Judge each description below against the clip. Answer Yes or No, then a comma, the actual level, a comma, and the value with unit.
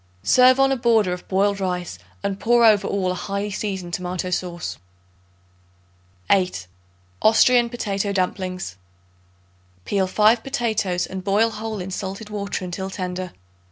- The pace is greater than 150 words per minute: No, slow, 135 wpm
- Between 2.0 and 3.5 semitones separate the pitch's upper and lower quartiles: Yes, average, 3.1 semitones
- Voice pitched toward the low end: No, high, 195 Hz